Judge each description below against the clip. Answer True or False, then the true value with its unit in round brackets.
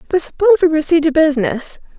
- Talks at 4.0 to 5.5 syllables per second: False (7.3 syllables/s)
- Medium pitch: False (315 Hz)